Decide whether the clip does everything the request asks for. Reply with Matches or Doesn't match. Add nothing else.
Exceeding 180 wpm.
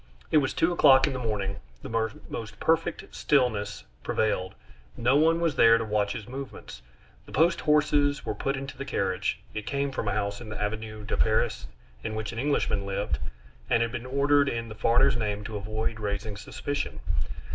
Matches